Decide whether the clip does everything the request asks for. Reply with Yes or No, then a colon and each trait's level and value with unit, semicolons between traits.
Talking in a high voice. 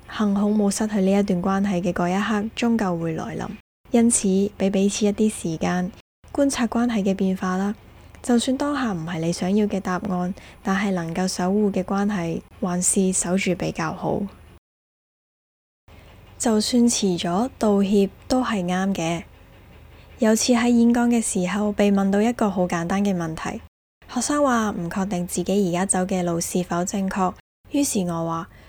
Yes: high, 195 Hz